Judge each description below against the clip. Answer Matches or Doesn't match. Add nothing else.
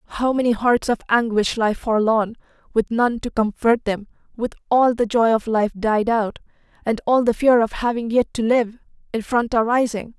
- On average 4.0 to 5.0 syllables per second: Matches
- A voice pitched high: Matches